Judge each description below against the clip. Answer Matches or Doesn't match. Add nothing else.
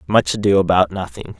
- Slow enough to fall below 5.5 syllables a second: Doesn't match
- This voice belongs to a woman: Doesn't match